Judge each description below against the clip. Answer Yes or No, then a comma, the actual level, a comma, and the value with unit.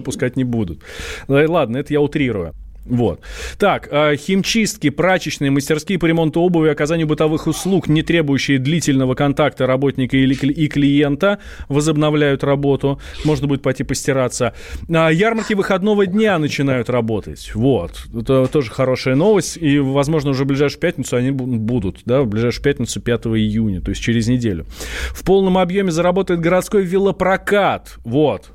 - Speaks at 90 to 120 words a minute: No, average, 140 wpm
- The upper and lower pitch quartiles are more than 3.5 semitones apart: Yes, average, 4.3 semitones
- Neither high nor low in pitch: Yes, medium, 145 Hz